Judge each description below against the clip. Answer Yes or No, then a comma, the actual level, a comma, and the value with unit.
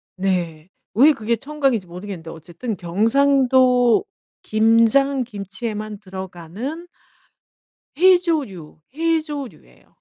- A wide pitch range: Yes, wide, 6.7 semitones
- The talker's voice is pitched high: Yes, high, 225 Hz